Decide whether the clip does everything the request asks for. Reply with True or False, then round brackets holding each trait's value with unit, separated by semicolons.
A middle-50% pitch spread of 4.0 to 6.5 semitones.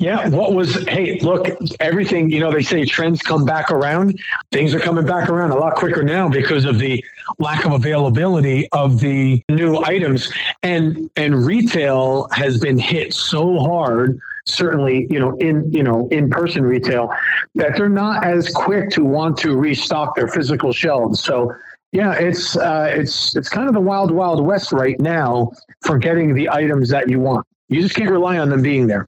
True (4.4 semitones)